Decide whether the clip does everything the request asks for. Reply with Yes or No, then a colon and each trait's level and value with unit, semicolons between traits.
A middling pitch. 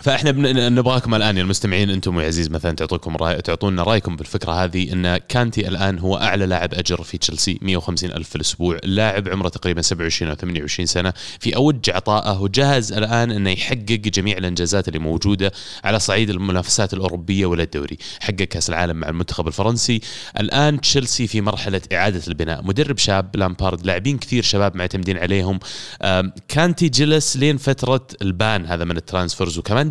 No: very low, 95 Hz